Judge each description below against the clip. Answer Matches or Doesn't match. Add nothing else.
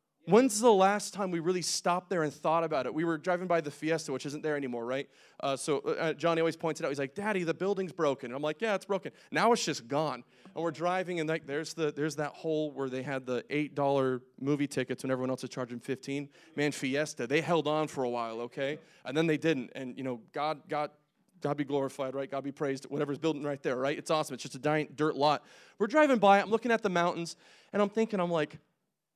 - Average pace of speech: Doesn't match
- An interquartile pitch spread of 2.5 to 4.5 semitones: Matches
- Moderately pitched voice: Matches